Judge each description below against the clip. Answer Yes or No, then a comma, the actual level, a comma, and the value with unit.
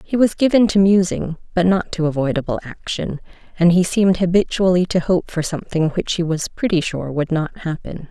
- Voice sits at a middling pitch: Yes, medium, 175 Hz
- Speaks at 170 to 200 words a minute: Yes, average, 195 wpm